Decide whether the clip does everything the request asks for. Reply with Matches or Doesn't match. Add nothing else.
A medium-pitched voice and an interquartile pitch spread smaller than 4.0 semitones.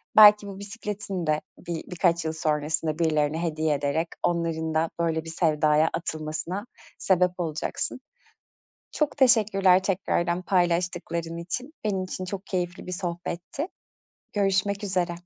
Matches